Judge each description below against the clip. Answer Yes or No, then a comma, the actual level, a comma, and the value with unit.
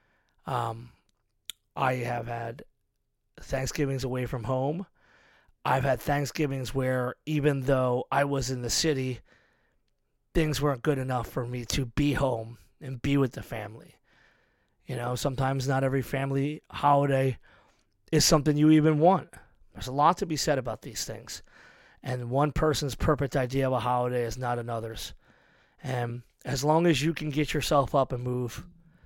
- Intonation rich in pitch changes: No, average, 2.9 semitones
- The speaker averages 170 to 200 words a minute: No, average, 155 wpm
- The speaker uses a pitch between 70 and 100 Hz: No, low, 135 Hz